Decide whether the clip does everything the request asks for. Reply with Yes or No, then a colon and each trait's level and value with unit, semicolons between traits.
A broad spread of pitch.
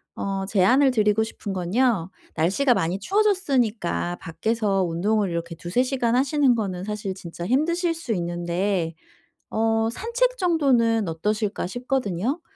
Yes: wide, 6.0 semitones